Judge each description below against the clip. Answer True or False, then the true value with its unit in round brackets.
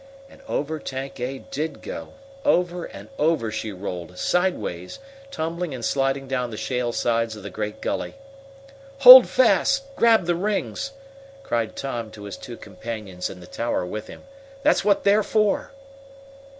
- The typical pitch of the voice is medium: False (130 Hz)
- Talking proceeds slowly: False (155 wpm)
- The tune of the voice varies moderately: False (8.6 semitones)